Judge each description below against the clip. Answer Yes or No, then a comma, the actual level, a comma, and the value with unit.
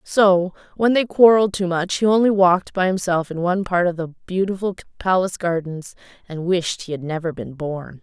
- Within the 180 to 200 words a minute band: Yes, average, 195 wpm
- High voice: No, medium, 180 Hz